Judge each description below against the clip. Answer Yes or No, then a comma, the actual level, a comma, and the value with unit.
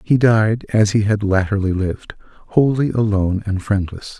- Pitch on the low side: Yes, low, 105 Hz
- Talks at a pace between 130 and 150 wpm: Yes, average, 145 wpm